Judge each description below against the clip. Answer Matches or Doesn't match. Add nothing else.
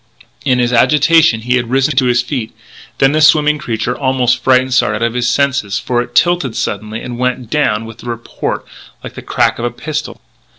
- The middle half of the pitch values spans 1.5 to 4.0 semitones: Matches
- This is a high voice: Doesn't match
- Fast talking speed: Matches